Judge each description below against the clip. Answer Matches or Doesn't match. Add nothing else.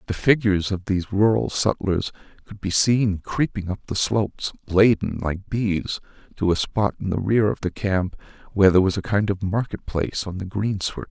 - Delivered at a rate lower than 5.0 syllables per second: Doesn't match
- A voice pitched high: Doesn't match